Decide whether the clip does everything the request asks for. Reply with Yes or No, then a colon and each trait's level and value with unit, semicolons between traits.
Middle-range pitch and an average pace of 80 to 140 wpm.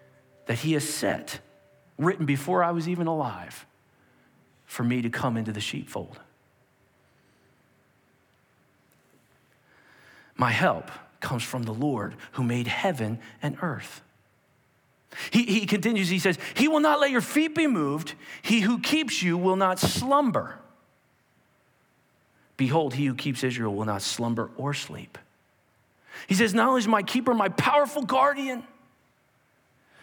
Yes: medium, 160 Hz; slow, 135 wpm